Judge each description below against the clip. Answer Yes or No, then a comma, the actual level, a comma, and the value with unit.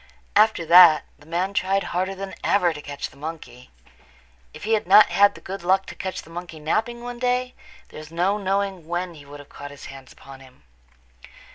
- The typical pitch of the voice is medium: Yes, medium, 180 Hz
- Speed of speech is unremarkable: No, fast, 210 wpm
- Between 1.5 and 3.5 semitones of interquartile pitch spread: No, average, 4.3 semitones